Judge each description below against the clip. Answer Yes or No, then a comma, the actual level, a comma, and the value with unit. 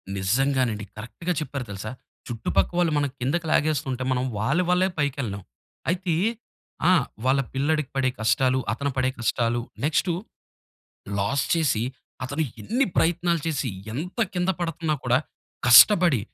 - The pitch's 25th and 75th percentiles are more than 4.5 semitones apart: Yes, average, 5.3 semitones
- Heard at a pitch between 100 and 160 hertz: Yes, medium, 140 Hz